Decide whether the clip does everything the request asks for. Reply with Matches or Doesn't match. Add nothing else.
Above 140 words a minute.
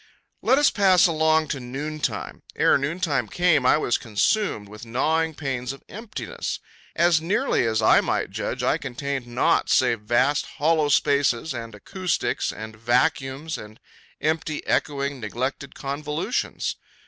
Doesn't match